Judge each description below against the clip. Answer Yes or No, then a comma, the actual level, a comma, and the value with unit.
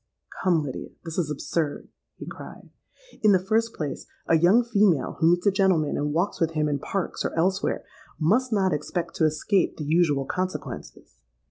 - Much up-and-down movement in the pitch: No, average, 4.2 semitones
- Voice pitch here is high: No, medium, 170 Hz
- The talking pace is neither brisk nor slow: Yes, average, 175 wpm